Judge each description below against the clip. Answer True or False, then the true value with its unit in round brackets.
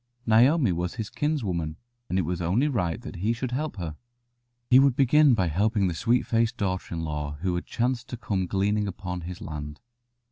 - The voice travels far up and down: True (5.8 semitones)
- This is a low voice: True (100 Hz)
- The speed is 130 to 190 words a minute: False (205 wpm)